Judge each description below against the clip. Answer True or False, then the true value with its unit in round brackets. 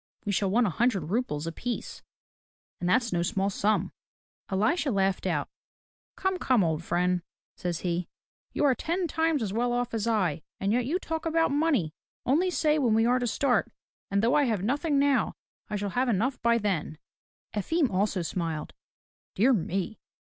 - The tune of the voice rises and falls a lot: True (6.1 semitones)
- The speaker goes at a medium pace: True (180 wpm)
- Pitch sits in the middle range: False (225 Hz)